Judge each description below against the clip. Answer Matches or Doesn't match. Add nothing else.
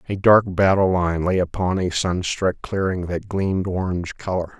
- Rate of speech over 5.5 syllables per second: Doesn't match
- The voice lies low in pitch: Matches